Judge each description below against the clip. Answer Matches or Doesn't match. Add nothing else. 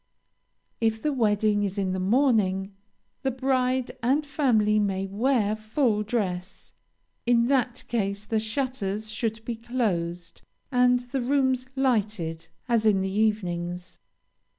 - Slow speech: Matches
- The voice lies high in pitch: Matches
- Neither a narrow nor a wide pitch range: Matches